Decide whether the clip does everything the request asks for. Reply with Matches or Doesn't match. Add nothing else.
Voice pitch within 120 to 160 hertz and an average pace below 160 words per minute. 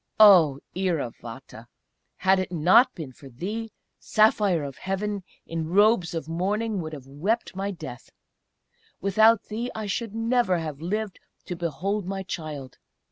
Doesn't match